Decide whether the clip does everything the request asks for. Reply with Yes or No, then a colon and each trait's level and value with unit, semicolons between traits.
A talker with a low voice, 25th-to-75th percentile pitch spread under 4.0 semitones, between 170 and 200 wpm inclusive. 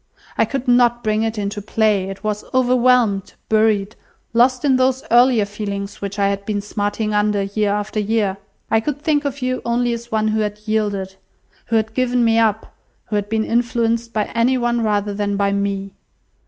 No: high, 220 Hz; average, 2.7 semitones; average, 190 wpm